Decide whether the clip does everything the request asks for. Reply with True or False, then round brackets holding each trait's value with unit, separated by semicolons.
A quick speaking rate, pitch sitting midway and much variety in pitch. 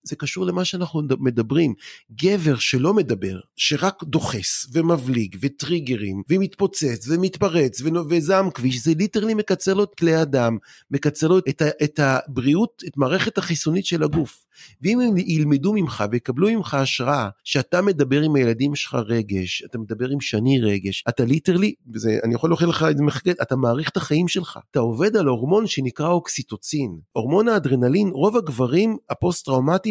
True (155 wpm; 150 Hz; 6.1 semitones)